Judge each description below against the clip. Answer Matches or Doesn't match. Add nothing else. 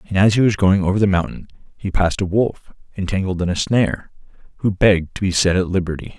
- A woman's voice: Doesn't match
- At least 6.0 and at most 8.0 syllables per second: Matches